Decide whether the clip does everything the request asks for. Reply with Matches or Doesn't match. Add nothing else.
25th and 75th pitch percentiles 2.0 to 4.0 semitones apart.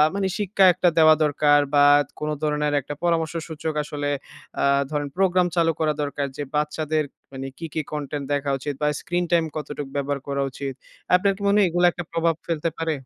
Matches